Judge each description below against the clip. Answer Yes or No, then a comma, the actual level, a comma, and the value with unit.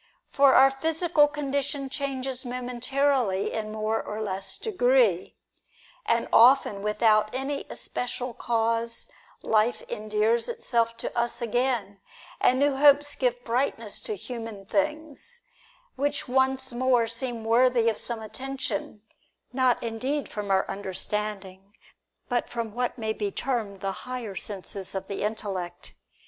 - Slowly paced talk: Yes, slow, 130 wpm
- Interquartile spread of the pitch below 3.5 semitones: No, average, 3.9 semitones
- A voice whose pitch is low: No, high, 235 Hz